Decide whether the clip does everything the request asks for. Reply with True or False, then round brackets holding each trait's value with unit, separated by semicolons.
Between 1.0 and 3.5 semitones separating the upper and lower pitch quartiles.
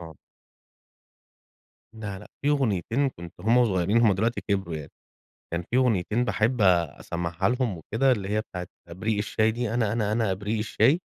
False (4.1 semitones)